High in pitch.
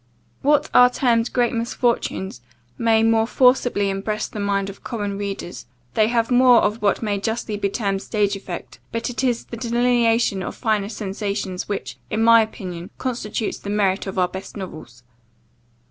Yes: high, 215 Hz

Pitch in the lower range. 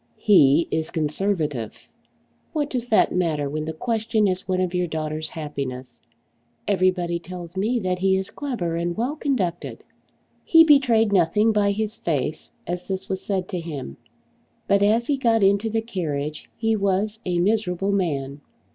No: medium, 185 Hz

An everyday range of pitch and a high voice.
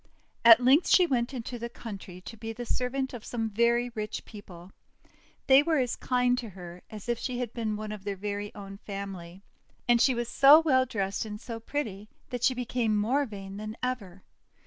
Yes: average, 3.5 semitones; high, 230 Hz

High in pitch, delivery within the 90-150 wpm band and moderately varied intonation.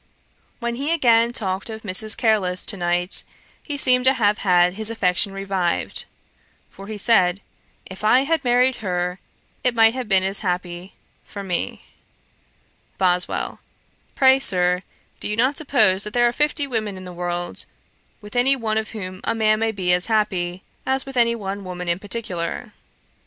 No: high, 210 Hz; average, 170 wpm; average, 4.5 semitones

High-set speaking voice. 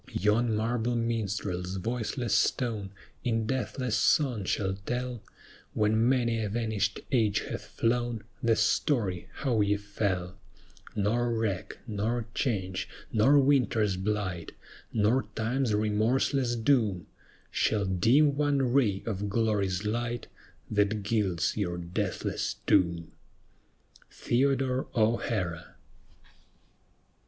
No: low, 110 Hz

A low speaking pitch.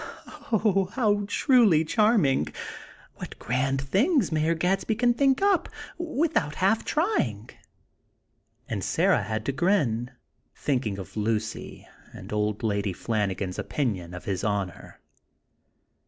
No: medium, 145 Hz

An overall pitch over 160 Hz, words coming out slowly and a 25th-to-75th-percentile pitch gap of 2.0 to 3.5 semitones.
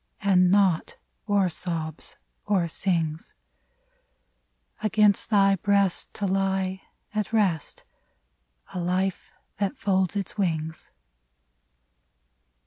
Yes: high, 190 Hz; slow, 95 wpm; average, 2.8 semitones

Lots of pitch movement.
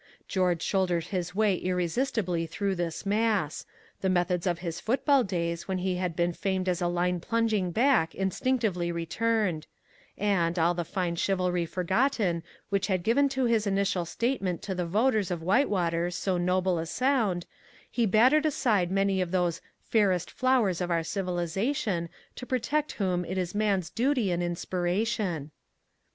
No: average, 3.8 semitones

